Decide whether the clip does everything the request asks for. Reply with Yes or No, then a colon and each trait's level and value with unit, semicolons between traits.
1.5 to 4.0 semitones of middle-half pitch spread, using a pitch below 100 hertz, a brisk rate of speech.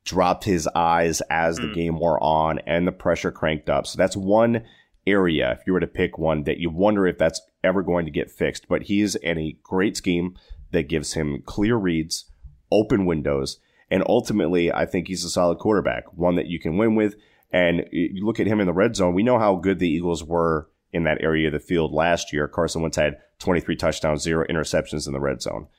Yes: narrow, 2.4 semitones; very low, 85 Hz; fast, 220 wpm